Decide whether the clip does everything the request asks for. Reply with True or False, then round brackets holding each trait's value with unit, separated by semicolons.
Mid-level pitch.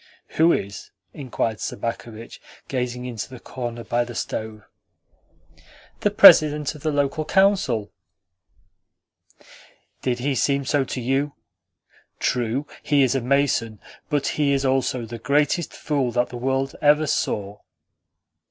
False (130 Hz)